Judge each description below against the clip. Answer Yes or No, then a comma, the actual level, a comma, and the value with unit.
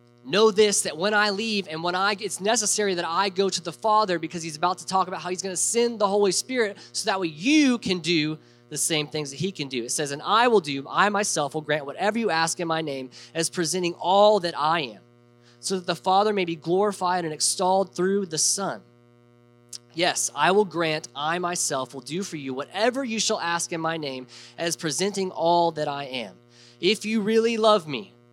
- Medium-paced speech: No, fast, 225 wpm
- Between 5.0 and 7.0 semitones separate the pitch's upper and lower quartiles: Yes, average, 5.3 semitones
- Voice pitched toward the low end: No, medium, 175 Hz